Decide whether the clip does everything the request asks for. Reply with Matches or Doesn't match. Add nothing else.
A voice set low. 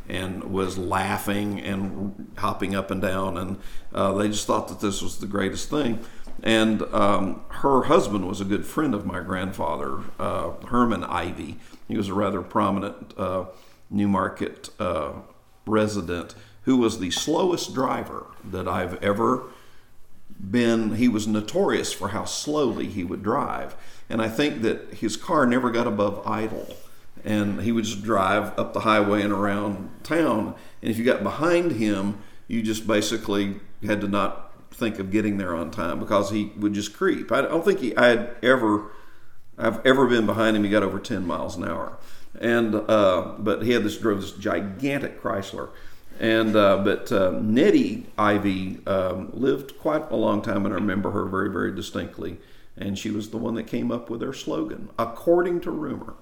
Matches